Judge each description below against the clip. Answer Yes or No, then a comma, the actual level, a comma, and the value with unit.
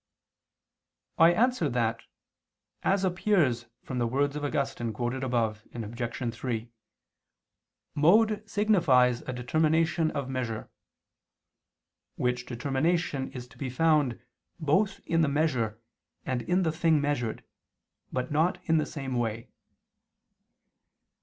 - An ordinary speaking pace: No, slow, 115 wpm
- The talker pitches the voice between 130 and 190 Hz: Yes, low, 135 Hz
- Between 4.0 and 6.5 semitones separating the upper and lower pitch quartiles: Yes, average, 5.0 semitones